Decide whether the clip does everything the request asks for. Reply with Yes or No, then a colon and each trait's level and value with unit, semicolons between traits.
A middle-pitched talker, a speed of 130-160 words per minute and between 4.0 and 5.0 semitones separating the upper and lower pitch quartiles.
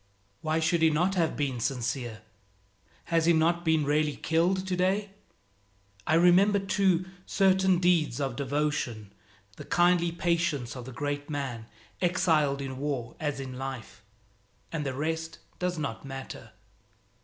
Yes: medium, 155 Hz; average, 140 wpm; average, 4.4 semitones